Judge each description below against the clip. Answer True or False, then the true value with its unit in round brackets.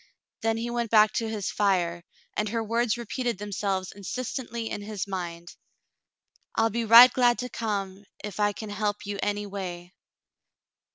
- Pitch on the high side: True (210 Hz)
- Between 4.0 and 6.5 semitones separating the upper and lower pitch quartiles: False (2.6 semitones)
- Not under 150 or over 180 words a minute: True (160 wpm)